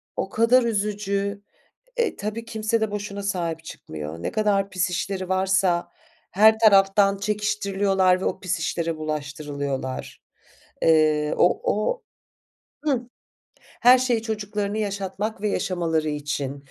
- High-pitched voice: Yes, high, 195 Hz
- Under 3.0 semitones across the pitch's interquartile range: No, average, 4.3 semitones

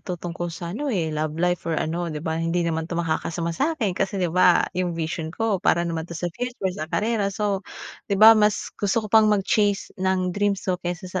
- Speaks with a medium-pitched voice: Yes, medium, 180 Hz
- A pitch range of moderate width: Yes, average, 3.4 semitones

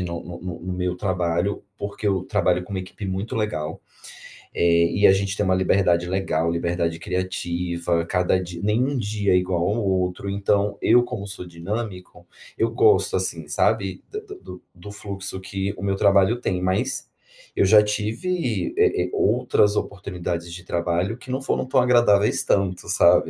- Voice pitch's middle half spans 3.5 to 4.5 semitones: No, average, 2.7 semitones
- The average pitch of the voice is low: Yes, very low, 95 Hz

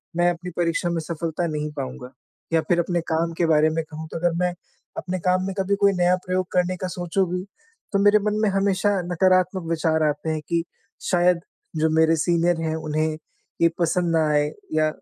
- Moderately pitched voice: Yes, medium, 170 Hz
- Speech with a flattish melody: Yes, narrow, 2.3 semitones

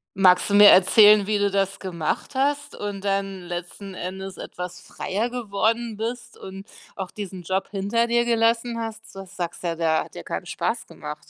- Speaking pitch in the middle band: No, high, 200 Hz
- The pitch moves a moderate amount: Yes, average, 3.2 semitones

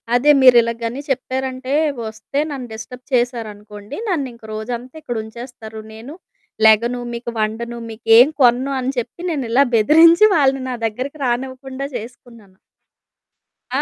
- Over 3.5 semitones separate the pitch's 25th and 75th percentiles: No, average, 2.8 semitones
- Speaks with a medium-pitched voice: No, high, 245 Hz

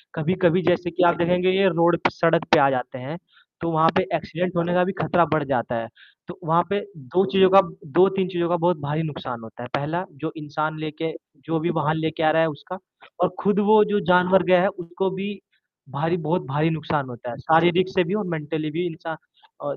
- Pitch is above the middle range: No, medium, 165 Hz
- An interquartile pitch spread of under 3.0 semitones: Yes, narrow, 2.6 semitones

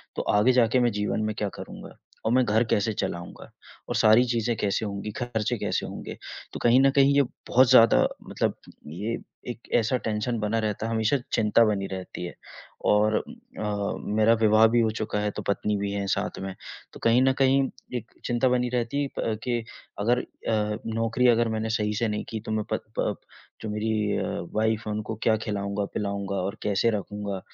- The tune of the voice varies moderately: No, narrow, 2.2 semitones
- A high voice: No, low, 110 Hz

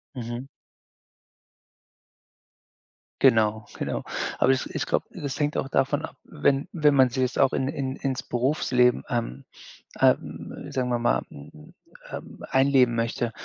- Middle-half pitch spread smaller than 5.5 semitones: Yes, narrow, 2.4 semitones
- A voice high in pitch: No, low, 130 Hz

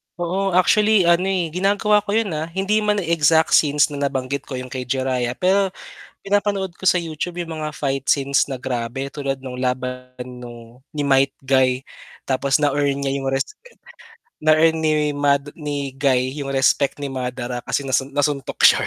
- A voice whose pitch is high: No, medium, 145 Hz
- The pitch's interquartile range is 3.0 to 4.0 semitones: No, average, 4.4 semitones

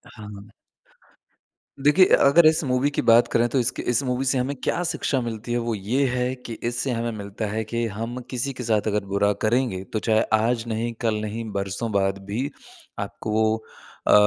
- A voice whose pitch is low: Yes, low, 115 Hz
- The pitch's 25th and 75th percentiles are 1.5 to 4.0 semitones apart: Yes, average, 2.8 semitones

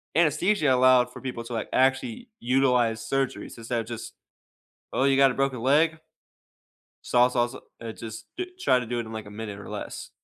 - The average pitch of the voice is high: No, low, 125 Hz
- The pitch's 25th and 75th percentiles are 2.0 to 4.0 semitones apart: Yes, average, 2.8 semitones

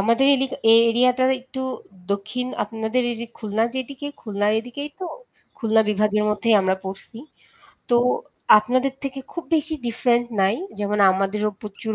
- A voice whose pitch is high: Yes, high, 230 Hz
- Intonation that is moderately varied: Yes, average, 3.3 semitones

